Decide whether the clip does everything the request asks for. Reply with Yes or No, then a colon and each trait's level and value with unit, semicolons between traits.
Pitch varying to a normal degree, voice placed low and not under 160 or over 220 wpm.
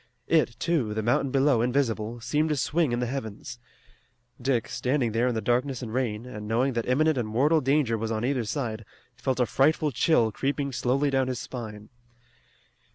Yes: average, 3.4 semitones; low, 125 Hz; average, 185 wpm